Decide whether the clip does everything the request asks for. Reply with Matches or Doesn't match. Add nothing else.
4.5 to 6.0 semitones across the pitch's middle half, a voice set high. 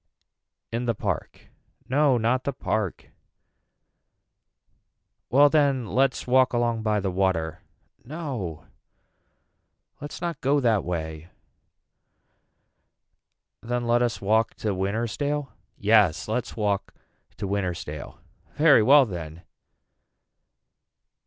Doesn't match